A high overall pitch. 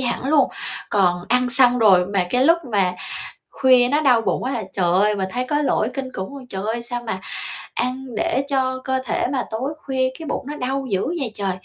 Yes: very high, 250 Hz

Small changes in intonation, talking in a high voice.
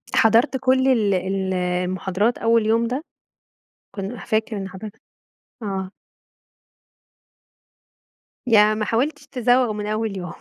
No: average, 3.4 semitones; high, 215 Hz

